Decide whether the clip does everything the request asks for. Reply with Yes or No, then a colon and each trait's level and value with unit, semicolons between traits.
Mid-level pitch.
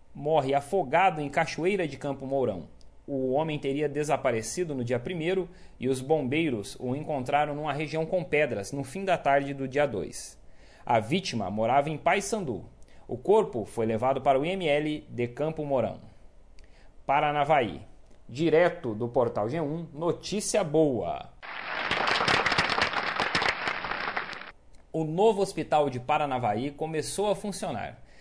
Yes: medium, 150 Hz